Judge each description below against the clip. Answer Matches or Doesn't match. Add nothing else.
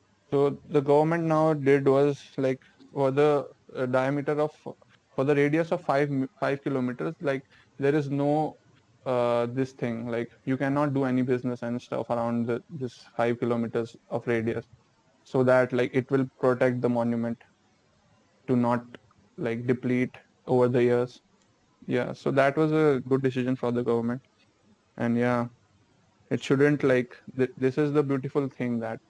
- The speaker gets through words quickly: Doesn't match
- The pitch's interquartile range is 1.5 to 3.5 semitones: Matches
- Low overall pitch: Matches